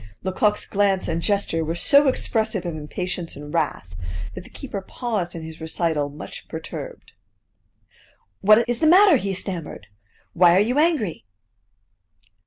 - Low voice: No, high, 190 Hz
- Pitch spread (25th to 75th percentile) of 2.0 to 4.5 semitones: No, average, 5.3 semitones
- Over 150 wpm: No, average, 145 wpm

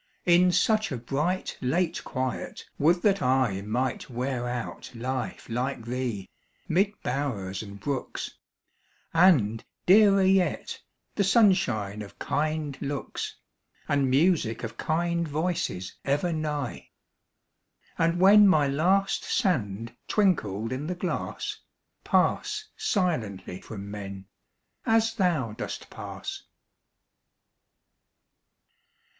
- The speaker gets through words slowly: Yes, slow, 105 wpm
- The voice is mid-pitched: Yes, medium, 145 Hz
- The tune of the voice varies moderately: No, wide, 7.6 semitones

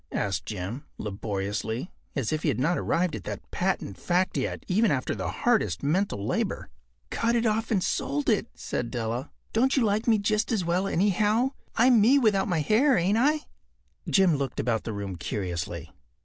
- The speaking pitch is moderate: Yes, medium, 175 Hz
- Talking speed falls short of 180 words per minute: No, average, 185 wpm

